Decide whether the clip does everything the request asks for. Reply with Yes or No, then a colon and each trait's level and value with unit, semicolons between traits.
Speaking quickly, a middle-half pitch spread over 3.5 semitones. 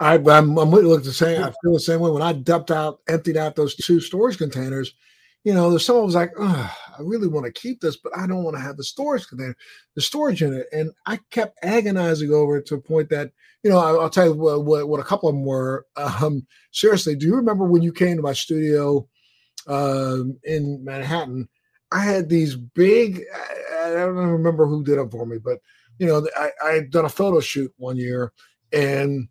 Yes: fast, 225 wpm; average, 4.0 semitones